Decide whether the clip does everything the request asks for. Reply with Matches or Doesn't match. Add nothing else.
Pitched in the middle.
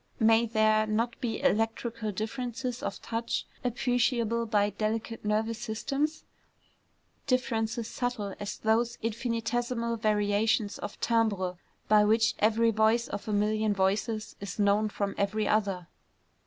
Doesn't match